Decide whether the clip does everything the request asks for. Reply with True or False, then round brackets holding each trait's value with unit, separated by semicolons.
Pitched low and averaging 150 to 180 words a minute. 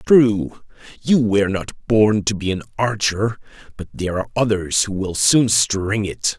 True (105 Hz; 170 wpm)